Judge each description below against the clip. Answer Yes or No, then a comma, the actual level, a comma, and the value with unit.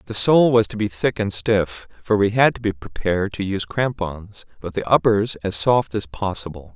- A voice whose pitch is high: No, low, 105 Hz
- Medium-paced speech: No, fast, 215 wpm